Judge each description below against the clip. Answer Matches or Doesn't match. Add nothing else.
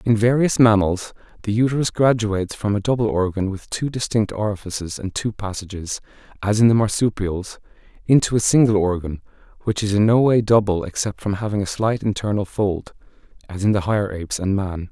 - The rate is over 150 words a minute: Matches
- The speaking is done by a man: Matches